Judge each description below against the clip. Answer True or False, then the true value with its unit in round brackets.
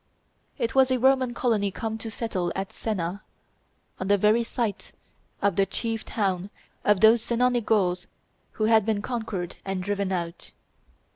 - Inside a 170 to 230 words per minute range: False (155 wpm)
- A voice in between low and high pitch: False (215 Hz)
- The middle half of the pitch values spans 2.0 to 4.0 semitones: True (3.1 semitones)